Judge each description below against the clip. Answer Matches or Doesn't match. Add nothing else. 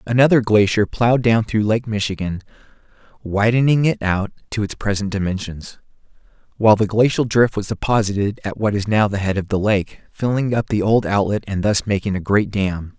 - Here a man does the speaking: Matches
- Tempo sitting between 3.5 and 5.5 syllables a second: Matches